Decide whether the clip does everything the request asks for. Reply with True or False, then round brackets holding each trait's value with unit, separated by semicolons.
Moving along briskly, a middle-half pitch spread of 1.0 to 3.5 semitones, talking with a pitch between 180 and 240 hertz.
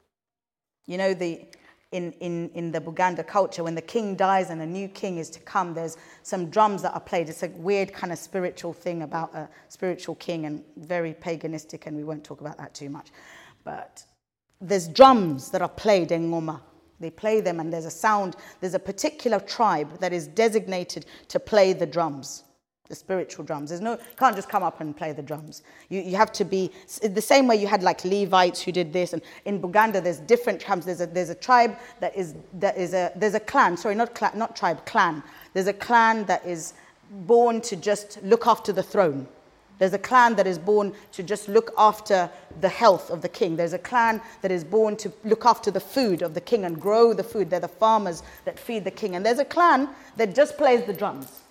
False (220 wpm; 4.1 semitones; 190 Hz)